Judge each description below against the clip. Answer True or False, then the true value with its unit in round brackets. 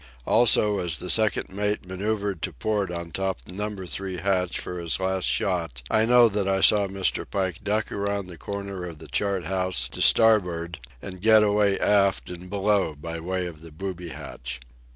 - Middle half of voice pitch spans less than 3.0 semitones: True (2.6 semitones)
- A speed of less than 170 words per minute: False (190 wpm)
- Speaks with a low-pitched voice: True (95 Hz)